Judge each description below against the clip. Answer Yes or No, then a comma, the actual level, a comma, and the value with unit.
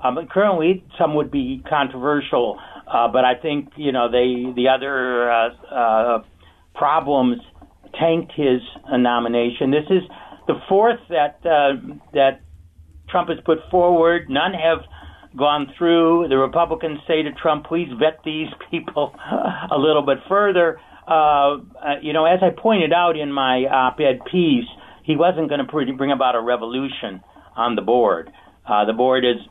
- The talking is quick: No, average, 155 wpm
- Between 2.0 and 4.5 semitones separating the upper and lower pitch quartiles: No, average, 4.9 semitones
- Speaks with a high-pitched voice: No, medium, 145 Hz